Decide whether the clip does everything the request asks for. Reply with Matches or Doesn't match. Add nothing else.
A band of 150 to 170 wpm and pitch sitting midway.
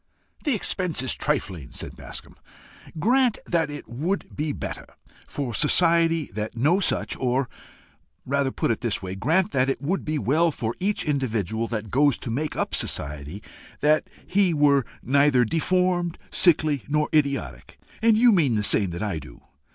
Matches